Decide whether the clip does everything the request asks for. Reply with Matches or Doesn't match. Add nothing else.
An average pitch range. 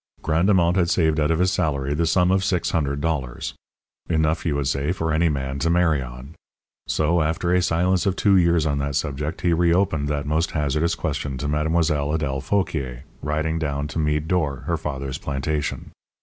Matches